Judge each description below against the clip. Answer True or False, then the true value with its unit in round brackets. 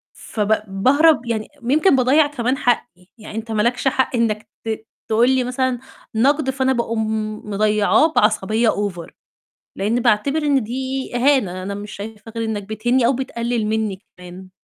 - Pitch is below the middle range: False (230 Hz)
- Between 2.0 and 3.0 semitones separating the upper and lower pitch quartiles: False (3.5 semitones)